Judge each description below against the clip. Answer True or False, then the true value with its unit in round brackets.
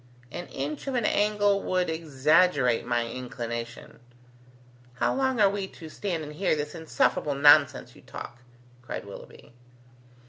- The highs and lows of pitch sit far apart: True (7.1 semitones)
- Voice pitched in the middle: True (155 Hz)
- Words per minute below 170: True (140 wpm)